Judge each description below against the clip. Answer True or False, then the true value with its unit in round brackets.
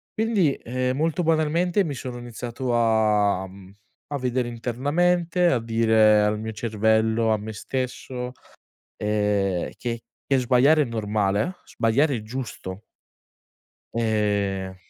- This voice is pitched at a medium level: False (115 Hz)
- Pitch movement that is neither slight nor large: True (3.9 semitones)